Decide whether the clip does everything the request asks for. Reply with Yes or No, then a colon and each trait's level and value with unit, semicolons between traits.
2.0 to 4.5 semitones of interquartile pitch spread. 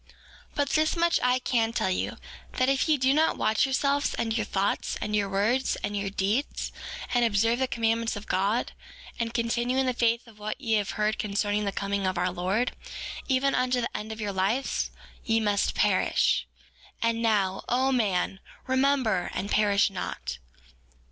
Yes: average, 4.0 semitones